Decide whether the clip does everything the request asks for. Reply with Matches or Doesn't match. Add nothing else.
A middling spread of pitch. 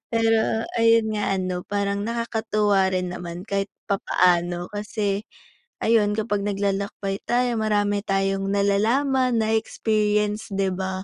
Doesn't match